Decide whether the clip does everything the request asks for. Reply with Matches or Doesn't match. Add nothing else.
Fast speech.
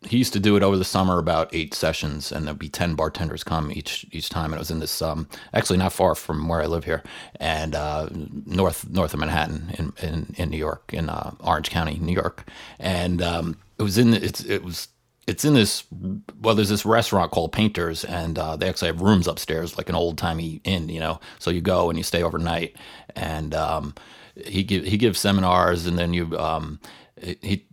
Matches